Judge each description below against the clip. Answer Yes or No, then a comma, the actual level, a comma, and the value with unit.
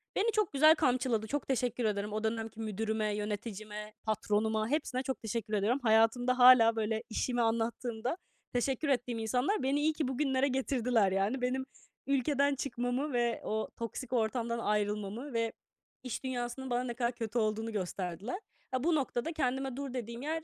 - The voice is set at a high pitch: Yes, high, 240 Hz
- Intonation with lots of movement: No, average, 3.2 semitones